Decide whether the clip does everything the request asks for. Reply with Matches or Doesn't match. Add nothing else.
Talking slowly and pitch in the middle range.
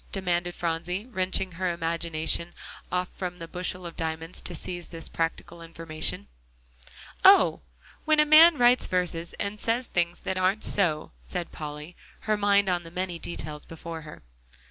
Doesn't match